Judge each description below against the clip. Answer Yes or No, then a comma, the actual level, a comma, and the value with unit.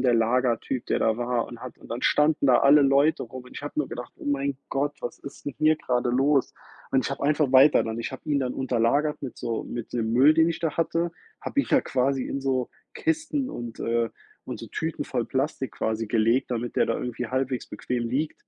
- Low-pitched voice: Yes, low, 130 Hz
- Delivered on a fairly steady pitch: No, average, 3.2 semitones